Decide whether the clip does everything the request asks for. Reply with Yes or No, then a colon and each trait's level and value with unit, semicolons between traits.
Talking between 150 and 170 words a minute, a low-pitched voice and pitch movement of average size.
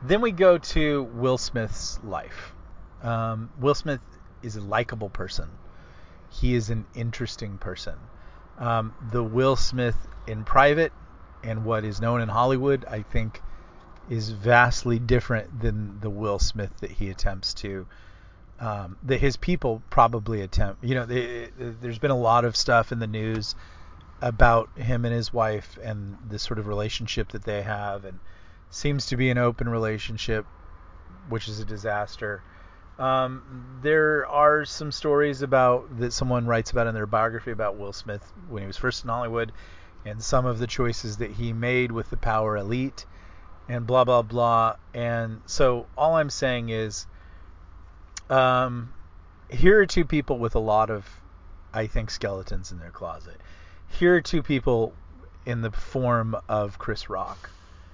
Yes: average, 160 wpm; low, 115 Hz; average, 4.4 semitones